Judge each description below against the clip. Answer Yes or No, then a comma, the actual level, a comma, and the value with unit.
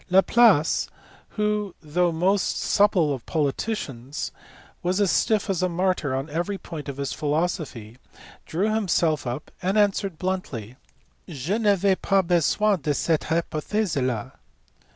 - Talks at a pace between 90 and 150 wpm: Yes, average, 140 wpm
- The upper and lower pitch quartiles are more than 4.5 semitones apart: Yes, average, 5.1 semitones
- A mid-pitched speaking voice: Yes, medium, 175 Hz